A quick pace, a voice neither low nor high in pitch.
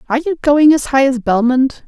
No: fast, 225 wpm; very high, 270 Hz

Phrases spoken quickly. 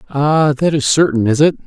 Yes: fast, 215 wpm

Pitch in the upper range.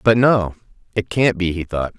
No: low, 100 Hz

